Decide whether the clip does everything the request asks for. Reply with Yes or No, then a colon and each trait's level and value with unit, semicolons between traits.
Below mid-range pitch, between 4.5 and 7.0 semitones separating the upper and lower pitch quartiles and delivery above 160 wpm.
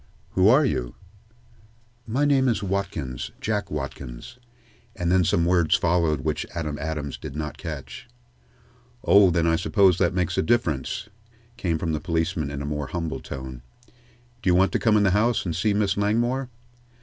Yes: very low, 85 Hz; average, 5.0 semitones; average, 175 wpm